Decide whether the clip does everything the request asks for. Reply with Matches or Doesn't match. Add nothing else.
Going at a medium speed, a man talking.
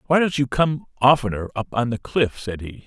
Doesn't match